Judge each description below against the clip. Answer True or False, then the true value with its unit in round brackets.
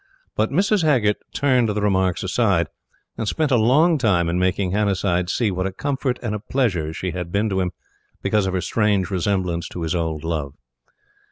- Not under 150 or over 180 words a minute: False (190 wpm)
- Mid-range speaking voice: False (100 Hz)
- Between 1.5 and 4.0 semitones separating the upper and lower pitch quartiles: False (4.5 semitones)